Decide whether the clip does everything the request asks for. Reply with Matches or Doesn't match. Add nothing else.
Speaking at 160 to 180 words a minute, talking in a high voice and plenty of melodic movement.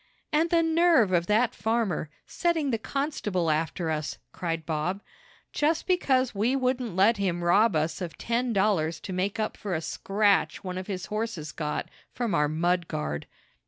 Matches